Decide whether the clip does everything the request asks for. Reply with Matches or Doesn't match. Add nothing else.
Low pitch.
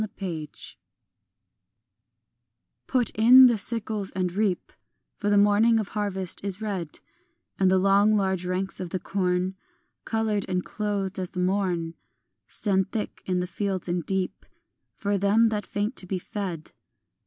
Doesn't match